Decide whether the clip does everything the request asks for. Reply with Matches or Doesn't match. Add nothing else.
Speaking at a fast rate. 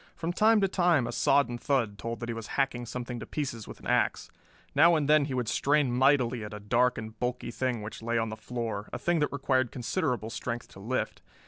Matches